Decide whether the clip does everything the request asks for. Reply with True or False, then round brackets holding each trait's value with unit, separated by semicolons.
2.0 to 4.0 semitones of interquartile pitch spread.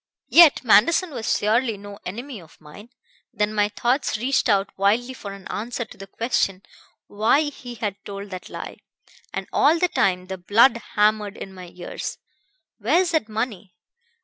True (3.7 semitones)